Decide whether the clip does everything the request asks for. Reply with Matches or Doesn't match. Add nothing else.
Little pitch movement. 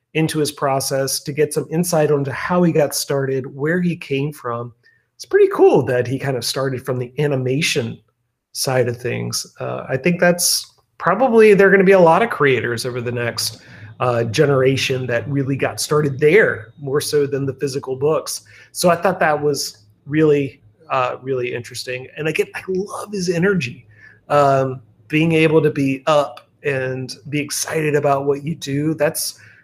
Doesn't match